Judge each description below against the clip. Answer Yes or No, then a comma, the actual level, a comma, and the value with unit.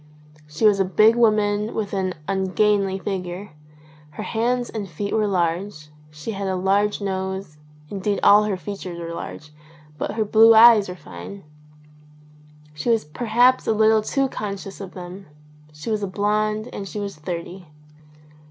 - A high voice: Yes, high, 200 Hz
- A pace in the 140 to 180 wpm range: Yes, average, 160 wpm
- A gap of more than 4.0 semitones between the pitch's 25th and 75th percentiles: No, average, 2.7 semitones